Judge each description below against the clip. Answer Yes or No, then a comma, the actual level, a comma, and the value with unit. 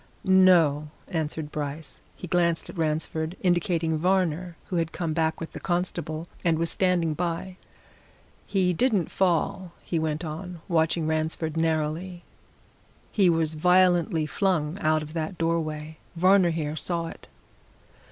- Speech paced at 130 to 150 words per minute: Yes, slow, 135 wpm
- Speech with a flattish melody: Yes, narrow, 2.3 semitones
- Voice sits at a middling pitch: Yes, medium, 165 Hz